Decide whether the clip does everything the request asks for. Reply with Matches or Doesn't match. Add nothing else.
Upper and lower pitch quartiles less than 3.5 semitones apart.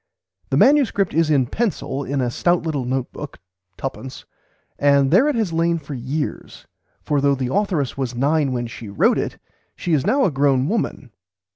Doesn't match